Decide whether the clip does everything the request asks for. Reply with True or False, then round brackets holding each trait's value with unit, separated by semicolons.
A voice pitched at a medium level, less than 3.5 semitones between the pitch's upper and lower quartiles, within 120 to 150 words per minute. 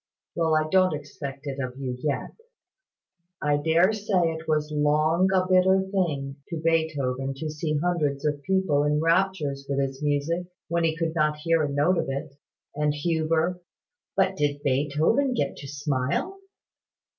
False (155 Hz; 3.0 semitones; 165 wpm)